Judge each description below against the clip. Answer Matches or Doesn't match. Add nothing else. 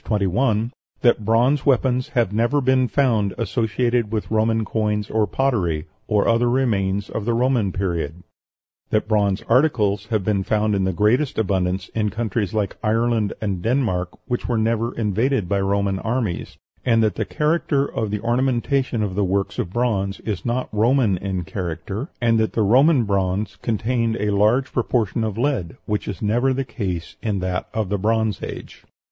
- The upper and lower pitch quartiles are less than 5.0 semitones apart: Matches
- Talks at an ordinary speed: Matches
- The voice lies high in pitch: Doesn't match